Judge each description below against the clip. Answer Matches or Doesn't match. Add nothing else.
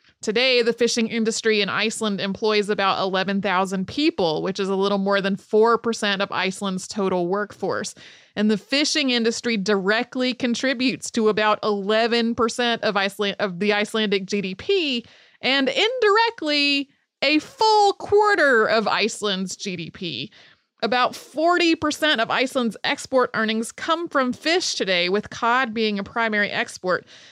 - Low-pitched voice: Doesn't match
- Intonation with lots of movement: Doesn't match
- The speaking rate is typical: Doesn't match